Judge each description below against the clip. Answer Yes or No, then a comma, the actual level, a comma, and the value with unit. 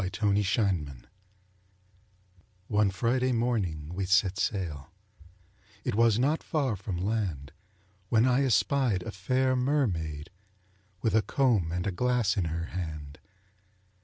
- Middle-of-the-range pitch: No, low, 100 Hz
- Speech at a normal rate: No, slow, 125 wpm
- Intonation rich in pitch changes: Yes, wide, 5.9 semitones